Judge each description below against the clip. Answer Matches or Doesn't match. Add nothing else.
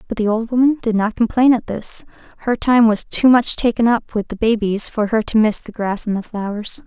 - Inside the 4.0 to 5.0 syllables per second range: Doesn't match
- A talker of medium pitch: Doesn't match